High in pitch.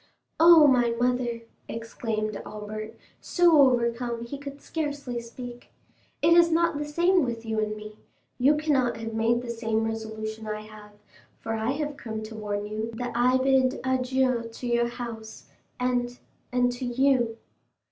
Yes: high, 240 Hz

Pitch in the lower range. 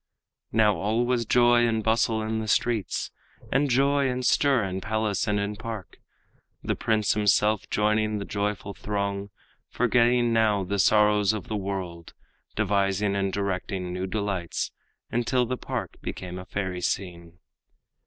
Yes: low, 105 Hz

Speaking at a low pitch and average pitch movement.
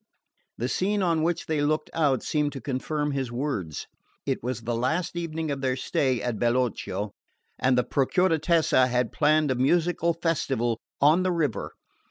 No: medium, 145 Hz; average, 4.5 semitones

